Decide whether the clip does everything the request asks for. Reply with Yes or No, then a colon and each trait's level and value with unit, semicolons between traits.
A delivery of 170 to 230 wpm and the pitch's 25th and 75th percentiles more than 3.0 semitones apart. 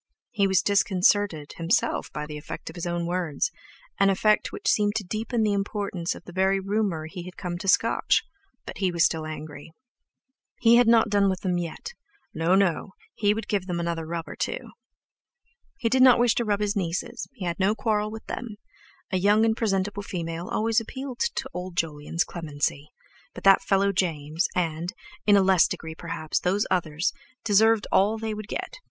Yes: average, 180 wpm; average, 3.9 semitones